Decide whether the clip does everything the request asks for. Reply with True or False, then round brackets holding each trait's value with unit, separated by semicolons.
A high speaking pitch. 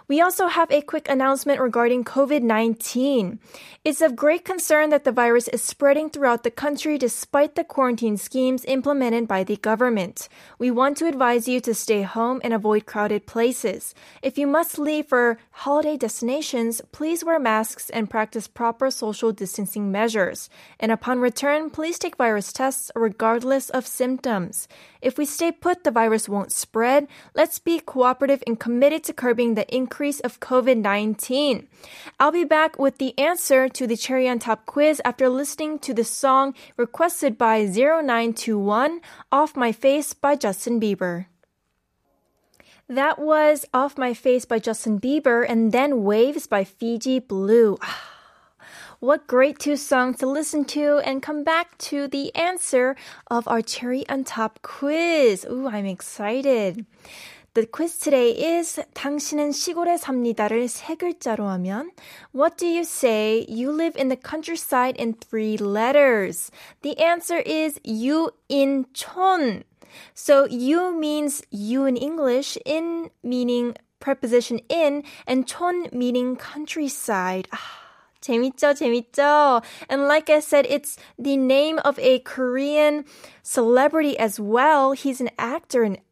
True (265 Hz)